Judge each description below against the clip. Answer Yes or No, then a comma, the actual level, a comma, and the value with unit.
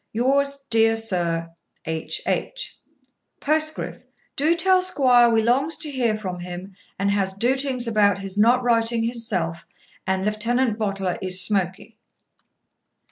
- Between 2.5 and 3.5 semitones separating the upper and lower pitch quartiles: No, average, 4.9 semitones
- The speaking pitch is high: Yes, high, 225 Hz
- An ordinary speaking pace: No, slow, 130 wpm